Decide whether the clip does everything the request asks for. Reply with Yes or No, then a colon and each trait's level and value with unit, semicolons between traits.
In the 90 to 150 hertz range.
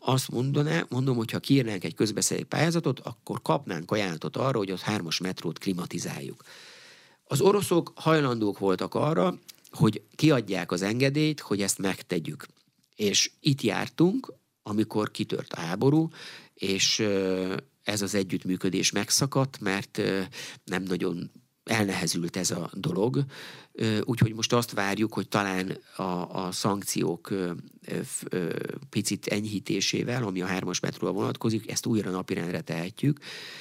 Yes: low, 110 Hz